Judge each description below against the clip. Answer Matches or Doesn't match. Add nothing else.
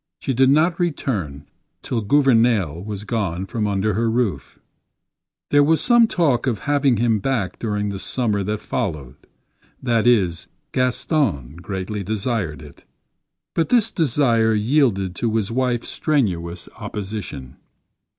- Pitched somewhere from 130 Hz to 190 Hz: Doesn't match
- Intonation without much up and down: Doesn't match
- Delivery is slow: Matches